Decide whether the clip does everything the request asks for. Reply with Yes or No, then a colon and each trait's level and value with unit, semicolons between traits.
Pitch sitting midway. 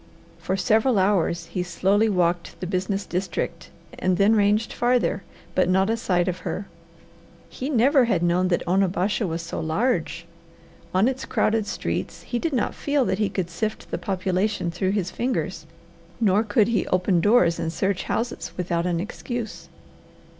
No: high, 195 Hz